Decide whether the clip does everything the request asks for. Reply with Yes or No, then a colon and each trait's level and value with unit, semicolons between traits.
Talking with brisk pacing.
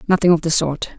Yes: fast, 245 wpm